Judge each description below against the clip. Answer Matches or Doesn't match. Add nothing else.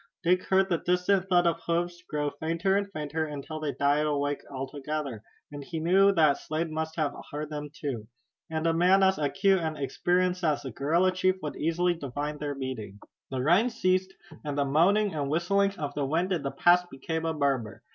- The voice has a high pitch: Doesn't match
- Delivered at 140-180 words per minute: Doesn't match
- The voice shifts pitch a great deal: Doesn't match